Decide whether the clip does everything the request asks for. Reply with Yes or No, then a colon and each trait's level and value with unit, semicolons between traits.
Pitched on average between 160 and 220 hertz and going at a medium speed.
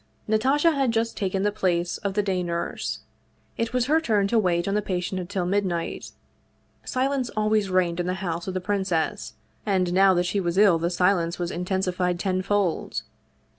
Yes: high, 190 Hz; average, 180 wpm